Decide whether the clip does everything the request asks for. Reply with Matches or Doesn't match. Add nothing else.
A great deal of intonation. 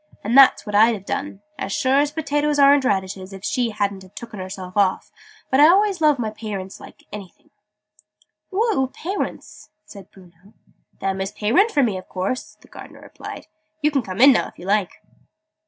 Matches